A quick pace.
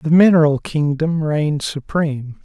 No: slow, 125 wpm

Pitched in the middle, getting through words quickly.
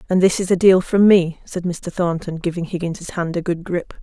Yes: medium, 175 Hz; fast, 240 wpm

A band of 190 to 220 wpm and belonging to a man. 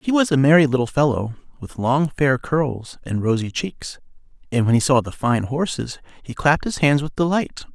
Yes: average, 200 wpm; male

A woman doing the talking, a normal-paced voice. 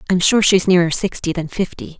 No: female; fast, 210 wpm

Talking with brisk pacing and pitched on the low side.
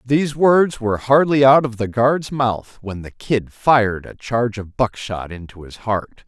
No: average, 190 wpm; low, 120 Hz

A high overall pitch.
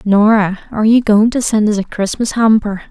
Yes: high, 215 Hz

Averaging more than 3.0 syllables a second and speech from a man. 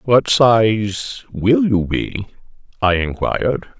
No: 2.9 syllables/s; male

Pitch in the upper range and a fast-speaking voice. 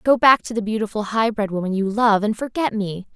Yes: high, 215 Hz; fast, 245 wpm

